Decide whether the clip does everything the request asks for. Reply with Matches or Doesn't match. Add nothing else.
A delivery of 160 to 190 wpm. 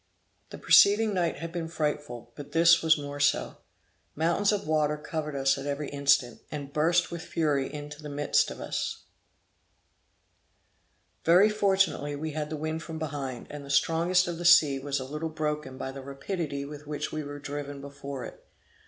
Matches